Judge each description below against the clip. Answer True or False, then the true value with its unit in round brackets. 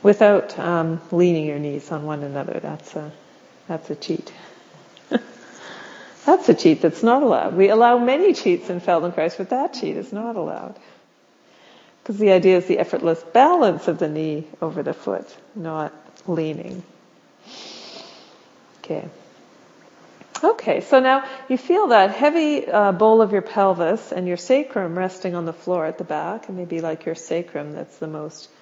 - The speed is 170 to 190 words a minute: False (160 wpm)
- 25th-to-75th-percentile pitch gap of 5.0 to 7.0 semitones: True (5.5 semitones)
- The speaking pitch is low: False (185 Hz)